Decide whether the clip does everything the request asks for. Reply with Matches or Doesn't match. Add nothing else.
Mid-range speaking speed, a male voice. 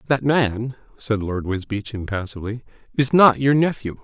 Matches